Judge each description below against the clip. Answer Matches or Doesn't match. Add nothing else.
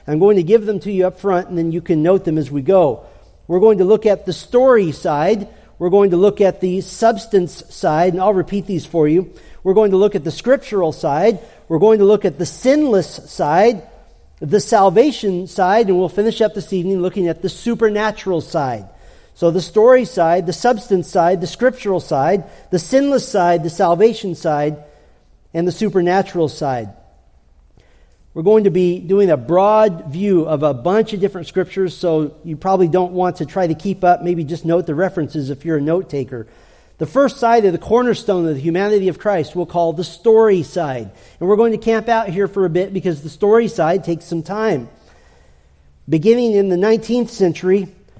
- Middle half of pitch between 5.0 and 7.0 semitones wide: Doesn't match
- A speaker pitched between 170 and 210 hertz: Matches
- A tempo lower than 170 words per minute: Doesn't match